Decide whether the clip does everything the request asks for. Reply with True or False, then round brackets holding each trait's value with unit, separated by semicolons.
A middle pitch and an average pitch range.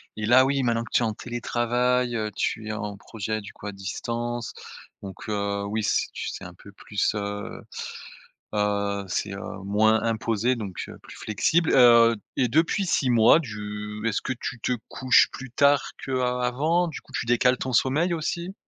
False (115 Hz; 3.4 semitones)